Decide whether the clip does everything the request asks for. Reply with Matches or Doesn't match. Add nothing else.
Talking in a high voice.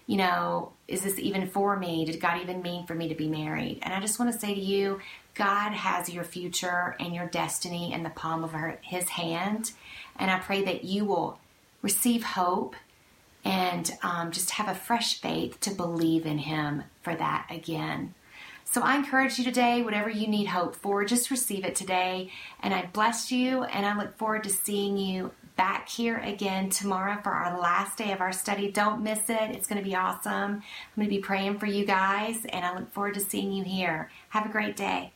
Matches